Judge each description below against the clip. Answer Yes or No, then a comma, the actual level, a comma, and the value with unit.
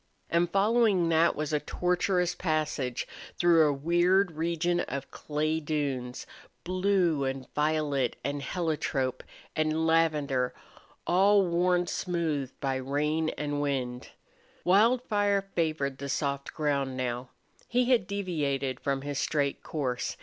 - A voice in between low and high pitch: Yes, medium, 155 Hz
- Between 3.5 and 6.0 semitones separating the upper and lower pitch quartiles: Yes, average, 4.2 semitones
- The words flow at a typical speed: No, slow, 120 wpm